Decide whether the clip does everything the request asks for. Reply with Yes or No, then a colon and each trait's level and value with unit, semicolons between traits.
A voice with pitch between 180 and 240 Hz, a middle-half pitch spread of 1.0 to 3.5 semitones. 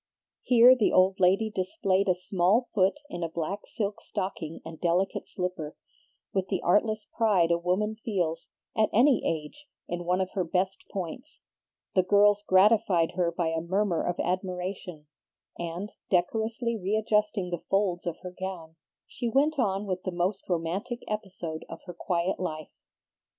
Yes: medium, 185 Hz; average, 3.2 semitones